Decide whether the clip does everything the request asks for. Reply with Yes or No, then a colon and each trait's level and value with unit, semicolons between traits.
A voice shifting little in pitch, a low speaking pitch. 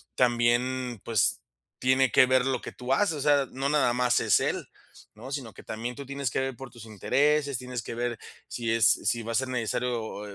Yes: narrow, 2.3 semitones; low, 125 Hz